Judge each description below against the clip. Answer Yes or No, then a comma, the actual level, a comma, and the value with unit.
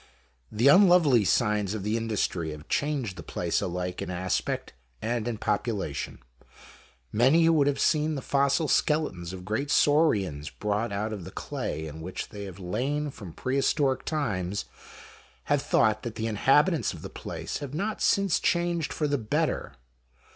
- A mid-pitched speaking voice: No, low, 115 Hz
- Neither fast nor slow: Yes, average, 160 wpm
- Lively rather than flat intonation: Yes, wide, 7.0 semitones